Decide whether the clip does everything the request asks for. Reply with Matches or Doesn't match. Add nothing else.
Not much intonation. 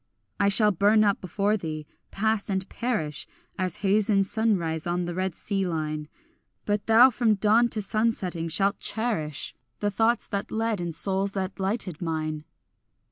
Doesn't match